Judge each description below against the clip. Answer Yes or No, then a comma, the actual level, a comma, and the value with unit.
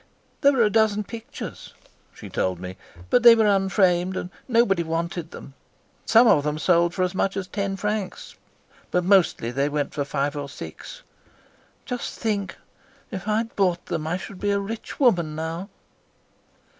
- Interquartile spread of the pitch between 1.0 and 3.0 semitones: No, average, 4.5 semitones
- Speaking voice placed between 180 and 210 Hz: Yes, high, 190 Hz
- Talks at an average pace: Yes, average, 170 wpm